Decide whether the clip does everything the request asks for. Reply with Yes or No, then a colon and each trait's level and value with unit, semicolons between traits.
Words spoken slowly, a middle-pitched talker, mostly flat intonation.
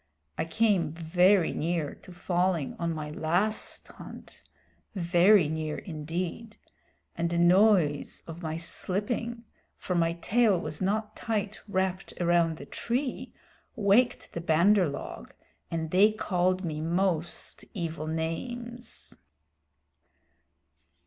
No: slow, 115 wpm; medium, 175 Hz; average, 4.0 semitones